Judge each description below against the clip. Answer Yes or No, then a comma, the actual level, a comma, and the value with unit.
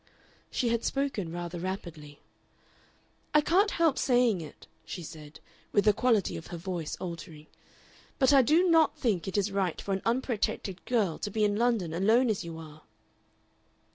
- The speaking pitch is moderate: No, high, 200 Hz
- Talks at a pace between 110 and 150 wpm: No, average, 170 wpm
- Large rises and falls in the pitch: Yes, wide, 6.3 semitones